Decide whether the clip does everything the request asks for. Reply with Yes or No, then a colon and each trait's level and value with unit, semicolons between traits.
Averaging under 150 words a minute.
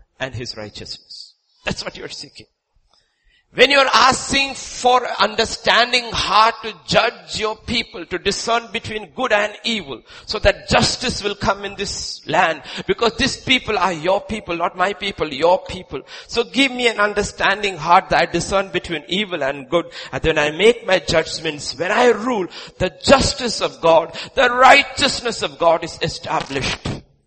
No: average, 165 wpm